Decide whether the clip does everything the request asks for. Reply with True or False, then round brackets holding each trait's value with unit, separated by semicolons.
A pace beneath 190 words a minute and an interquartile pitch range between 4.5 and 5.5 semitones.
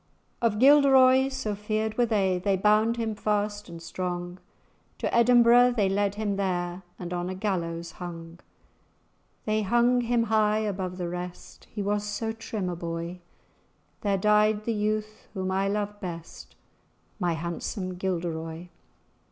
False (145 wpm; 3.4 semitones)